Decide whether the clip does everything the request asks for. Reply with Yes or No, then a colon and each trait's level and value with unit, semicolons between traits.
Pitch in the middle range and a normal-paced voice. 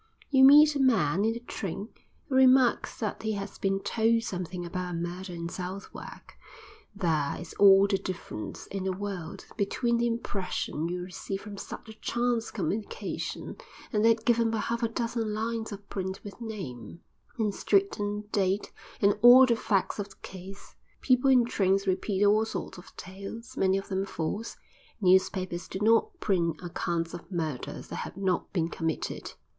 No: high, 200 Hz; average, 170 wpm